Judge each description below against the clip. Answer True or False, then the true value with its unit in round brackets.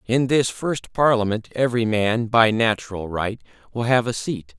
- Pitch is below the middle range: True (115 Hz)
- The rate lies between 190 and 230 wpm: False (170 wpm)